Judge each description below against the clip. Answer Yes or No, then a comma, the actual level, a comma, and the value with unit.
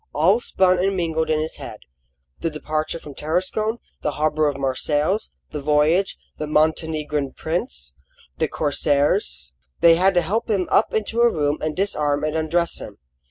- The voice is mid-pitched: Yes, medium, 155 Hz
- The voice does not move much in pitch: No, average, 3.5 semitones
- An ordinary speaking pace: Yes, average, 160 wpm